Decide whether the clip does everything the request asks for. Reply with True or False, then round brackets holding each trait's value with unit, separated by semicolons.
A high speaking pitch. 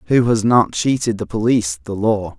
False (110 Hz)